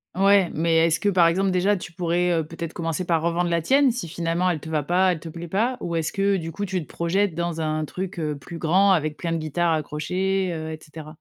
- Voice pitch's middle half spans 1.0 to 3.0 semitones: Yes, average, 2.7 semitones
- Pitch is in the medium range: Yes, medium, 170 Hz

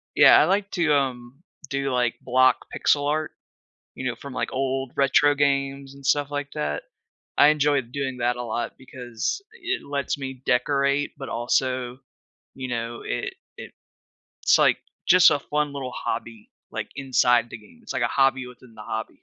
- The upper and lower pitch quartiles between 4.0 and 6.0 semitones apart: No, average, 2.7 semitones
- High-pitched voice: No, low, 135 Hz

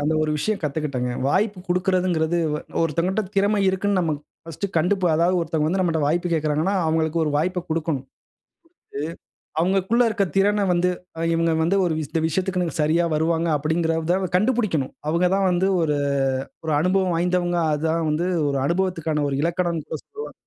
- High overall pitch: No, medium, 170 Hz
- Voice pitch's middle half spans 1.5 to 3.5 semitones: Yes, average, 2.8 semitones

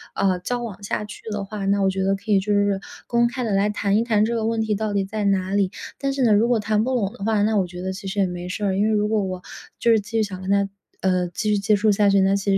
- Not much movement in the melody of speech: Yes, narrow, 2.0 semitones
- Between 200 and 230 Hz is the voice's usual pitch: Yes, high, 205 Hz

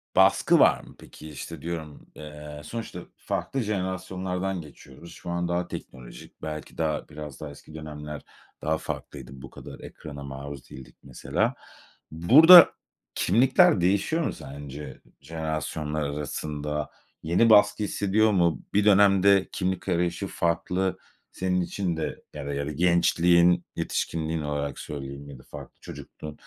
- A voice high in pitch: No, very low, 80 Hz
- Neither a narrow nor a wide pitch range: Yes, average, 3.9 semitones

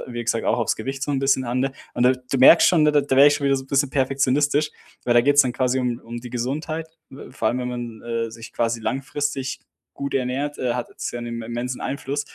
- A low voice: Yes, low, 130 Hz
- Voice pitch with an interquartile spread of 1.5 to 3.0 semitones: Yes, average, 2.7 semitones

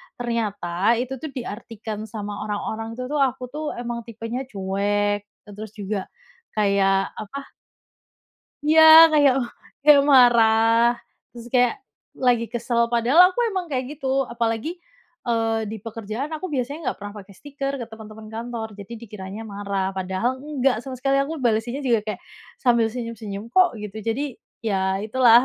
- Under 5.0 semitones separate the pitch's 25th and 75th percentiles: Yes, average, 3.4 semitones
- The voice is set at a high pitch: Yes, high, 230 Hz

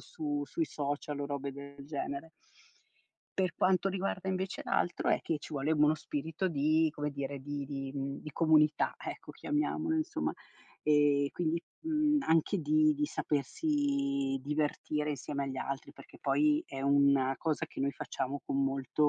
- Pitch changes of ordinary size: Yes, average, 4.1 semitones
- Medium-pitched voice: Yes, medium, 150 Hz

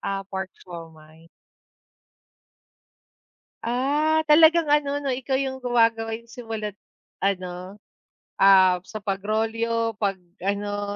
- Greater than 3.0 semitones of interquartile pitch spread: Yes, average, 4.7 semitones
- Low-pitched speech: No, high, 220 Hz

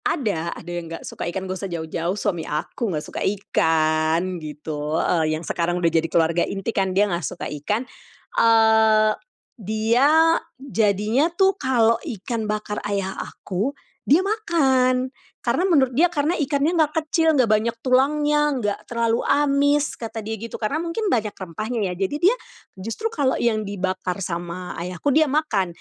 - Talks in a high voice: Yes, high, 215 Hz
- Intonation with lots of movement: Yes, wide, 7.5 semitones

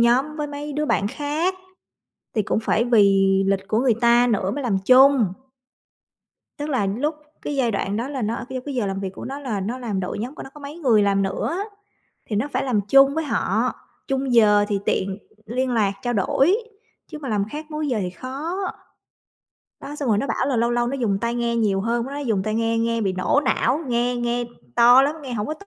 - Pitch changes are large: No, average, 4.9 semitones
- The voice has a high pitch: Yes, high, 240 Hz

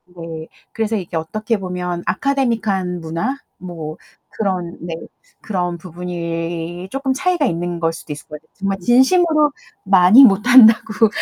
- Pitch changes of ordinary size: Yes, average, 5.0 semitones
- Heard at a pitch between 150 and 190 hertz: Yes, medium, 185 Hz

